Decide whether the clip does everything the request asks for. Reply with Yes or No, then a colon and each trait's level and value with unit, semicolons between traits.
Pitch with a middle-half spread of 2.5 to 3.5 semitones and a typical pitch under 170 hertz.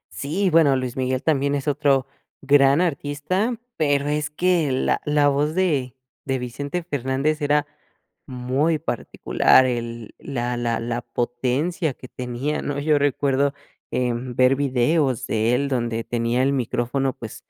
Yes: average, 3.1 semitones; low, 135 Hz